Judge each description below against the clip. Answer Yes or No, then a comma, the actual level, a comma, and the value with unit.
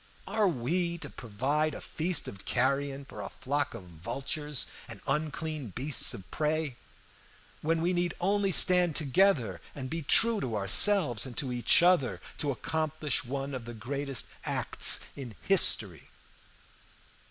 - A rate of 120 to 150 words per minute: Yes, average, 145 wpm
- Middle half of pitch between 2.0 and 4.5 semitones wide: No, average, 5.0 semitones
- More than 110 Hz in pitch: Yes, medium, 140 Hz